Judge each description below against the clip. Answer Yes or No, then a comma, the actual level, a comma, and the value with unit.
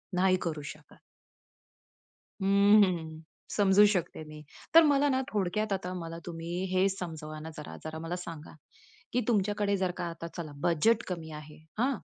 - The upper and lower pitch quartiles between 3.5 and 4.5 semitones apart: Yes, average, 4.2 semitones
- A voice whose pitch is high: No, medium, 180 Hz